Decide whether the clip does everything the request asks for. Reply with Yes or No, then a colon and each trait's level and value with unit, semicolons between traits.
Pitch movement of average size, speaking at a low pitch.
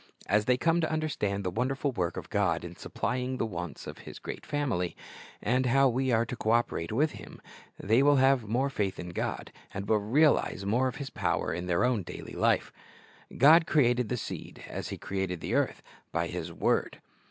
No: wide, 5.9 semitones; low, 120 Hz